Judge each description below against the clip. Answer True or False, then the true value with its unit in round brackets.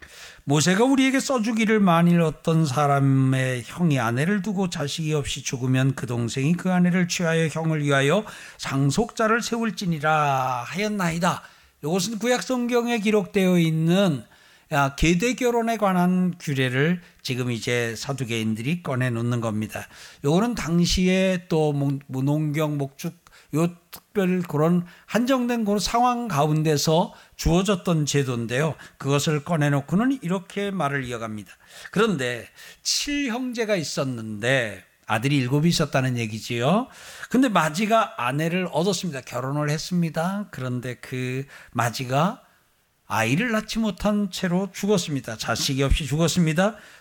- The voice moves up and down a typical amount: False (6.4 semitones)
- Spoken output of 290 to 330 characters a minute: True (295 characters per minute)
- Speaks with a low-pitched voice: False (160 Hz)